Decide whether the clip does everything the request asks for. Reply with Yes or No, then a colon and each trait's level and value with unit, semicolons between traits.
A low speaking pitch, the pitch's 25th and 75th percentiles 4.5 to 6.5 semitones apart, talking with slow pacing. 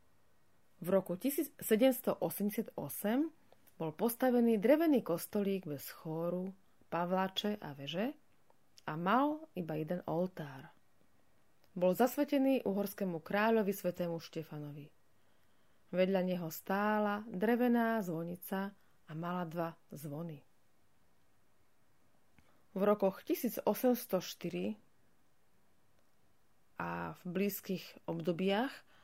No: medium, 185 Hz; average, 5.2 semitones; slow, 80 wpm